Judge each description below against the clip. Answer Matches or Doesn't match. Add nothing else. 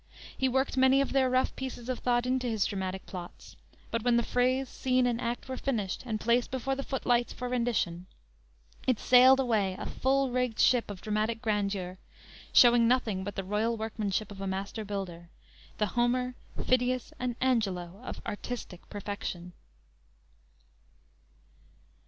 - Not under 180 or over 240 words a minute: Doesn't match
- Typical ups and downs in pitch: Matches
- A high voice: Matches